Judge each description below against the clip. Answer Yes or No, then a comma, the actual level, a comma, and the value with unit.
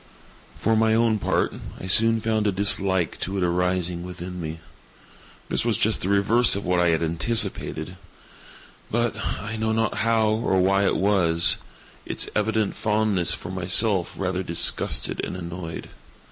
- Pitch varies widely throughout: No, average, 3.5 semitones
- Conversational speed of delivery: Yes, average, 145 wpm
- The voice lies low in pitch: Yes, very low, 95 Hz